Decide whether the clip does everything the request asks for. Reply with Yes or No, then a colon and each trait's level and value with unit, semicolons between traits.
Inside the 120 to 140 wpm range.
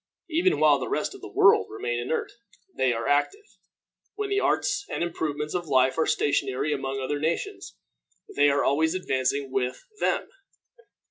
No: average, 160 wpm